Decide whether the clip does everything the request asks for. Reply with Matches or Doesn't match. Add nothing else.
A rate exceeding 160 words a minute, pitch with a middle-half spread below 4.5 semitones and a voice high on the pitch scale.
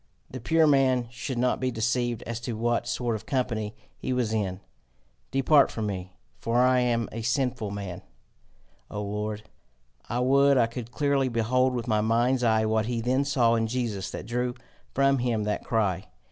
Doesn't match